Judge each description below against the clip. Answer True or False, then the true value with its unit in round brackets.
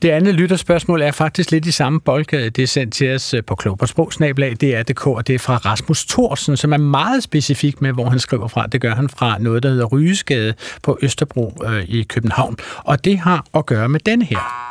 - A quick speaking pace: False (215 wpm)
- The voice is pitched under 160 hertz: True (140 Hz)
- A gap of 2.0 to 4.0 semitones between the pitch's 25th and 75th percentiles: False (4.4 semitones)